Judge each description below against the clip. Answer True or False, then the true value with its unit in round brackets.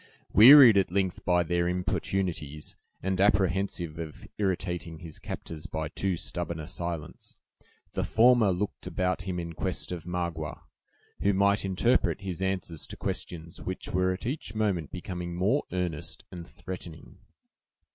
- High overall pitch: False (90 Hz)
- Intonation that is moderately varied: False (2.3 semitones)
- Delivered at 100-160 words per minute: True (145 wpm)